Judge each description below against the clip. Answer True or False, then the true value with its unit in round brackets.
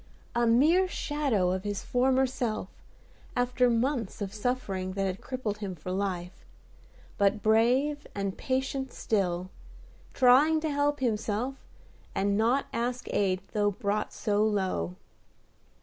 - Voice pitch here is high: True (220 Hz)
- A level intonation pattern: False (4.7 semitones)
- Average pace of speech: False (130 wpm)